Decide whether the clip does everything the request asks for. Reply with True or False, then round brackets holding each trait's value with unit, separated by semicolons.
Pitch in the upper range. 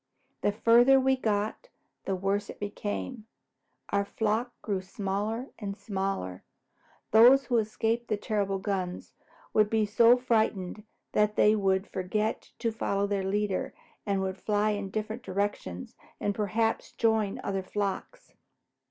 True (210 Hz)